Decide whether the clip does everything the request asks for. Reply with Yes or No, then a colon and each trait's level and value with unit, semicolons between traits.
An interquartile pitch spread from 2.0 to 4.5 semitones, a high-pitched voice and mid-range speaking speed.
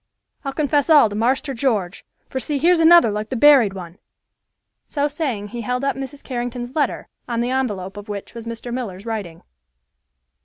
No: average, 4.9 semitones; high, 245 Hz; average, 180 wpm